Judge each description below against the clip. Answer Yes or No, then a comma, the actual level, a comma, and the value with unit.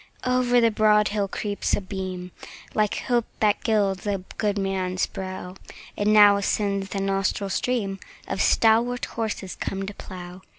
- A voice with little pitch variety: Yes, narrow, 1.9 semitones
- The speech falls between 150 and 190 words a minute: Yes, average, 160 wpm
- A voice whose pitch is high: Yes, high, 200 Hz